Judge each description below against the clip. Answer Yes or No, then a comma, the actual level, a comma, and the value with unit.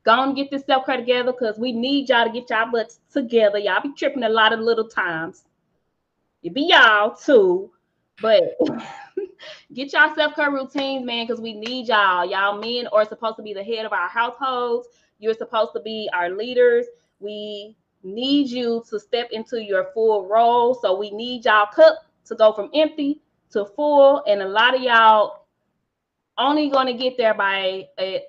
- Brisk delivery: No, average, 190 wpm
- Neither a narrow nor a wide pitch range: Yes, average, 4.2 semitones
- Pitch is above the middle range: Yes, high, 235 Hz